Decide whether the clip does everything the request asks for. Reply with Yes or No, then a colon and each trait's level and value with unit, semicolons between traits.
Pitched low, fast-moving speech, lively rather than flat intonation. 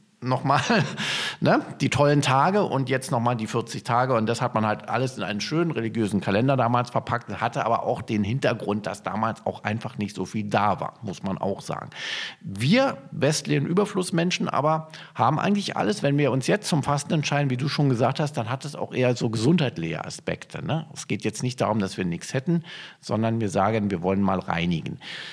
Yes: low, 130 Hz; fast, 205 wpm; wide, 5.7 semitones